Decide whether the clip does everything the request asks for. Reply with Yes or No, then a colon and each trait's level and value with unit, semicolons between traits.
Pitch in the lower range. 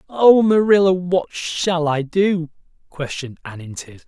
No: medium, 170 Hz